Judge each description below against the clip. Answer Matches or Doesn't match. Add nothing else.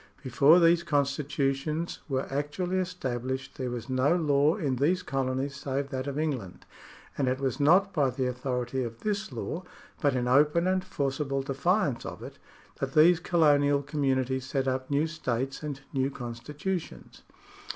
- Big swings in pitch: Doesn't match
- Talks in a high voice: Doesn't match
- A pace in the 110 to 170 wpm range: Matches